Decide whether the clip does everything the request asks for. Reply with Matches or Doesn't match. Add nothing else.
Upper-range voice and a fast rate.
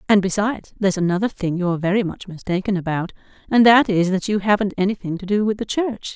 Matches